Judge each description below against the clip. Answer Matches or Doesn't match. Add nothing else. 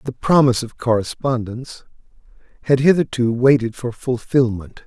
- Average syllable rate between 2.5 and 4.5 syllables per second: Doesn't match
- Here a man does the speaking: Matches